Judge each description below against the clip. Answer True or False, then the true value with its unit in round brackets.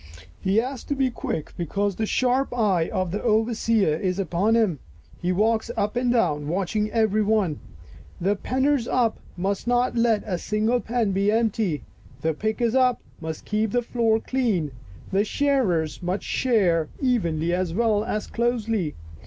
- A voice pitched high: True (215 Hz)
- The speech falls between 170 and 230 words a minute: True (175 wpm)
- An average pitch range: True (4.5 semitones)